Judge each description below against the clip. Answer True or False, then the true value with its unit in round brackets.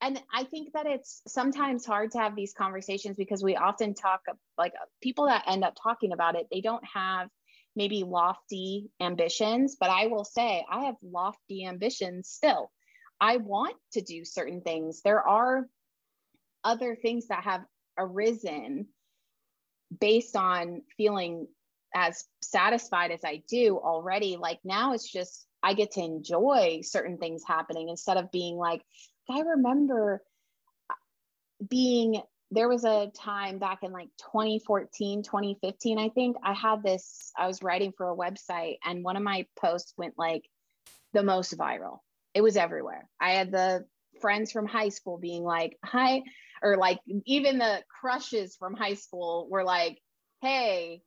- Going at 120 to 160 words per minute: True (155 wpm)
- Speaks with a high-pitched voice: True (200 Hz)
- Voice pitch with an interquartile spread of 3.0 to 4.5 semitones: True (4.2 semitones)